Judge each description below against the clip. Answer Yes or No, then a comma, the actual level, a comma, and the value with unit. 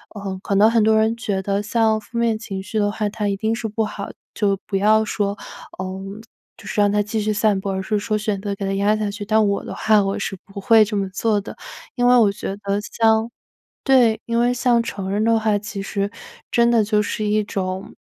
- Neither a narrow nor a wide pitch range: No, narrow, 1.7 semitones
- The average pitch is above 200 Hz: Yes, high, 210 Hz